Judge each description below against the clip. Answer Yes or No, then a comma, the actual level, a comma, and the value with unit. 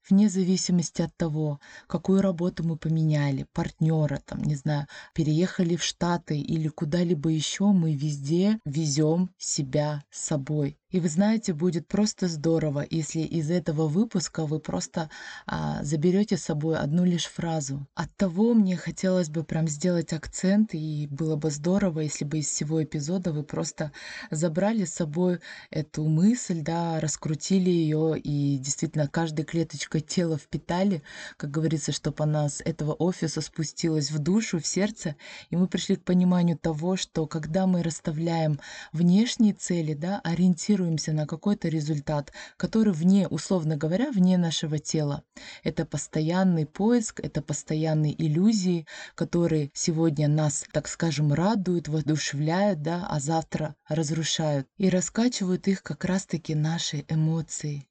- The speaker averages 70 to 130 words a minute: No, average, 140 wpm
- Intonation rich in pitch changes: No, average, 2.9 semitones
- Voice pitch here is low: No, medium, 165 Hz